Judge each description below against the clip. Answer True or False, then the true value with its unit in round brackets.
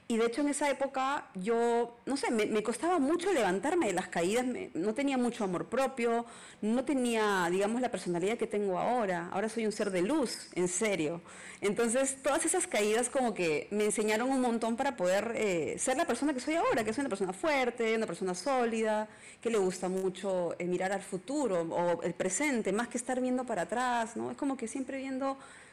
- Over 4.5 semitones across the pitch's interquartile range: True (5.0 semitones)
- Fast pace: True (210 wpm)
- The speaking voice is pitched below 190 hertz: False (230 Hz)